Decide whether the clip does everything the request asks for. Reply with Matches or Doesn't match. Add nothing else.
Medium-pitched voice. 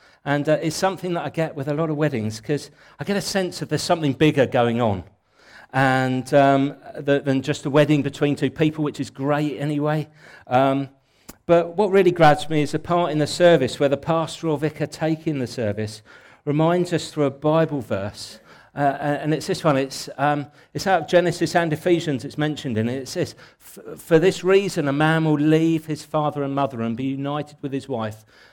Matches